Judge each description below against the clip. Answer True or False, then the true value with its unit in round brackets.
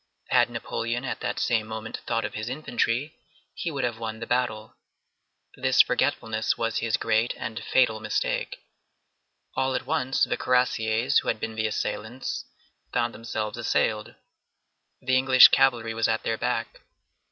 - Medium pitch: False (115 Hz)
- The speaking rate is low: False (150 wpm)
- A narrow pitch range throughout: True (2.3 semitones)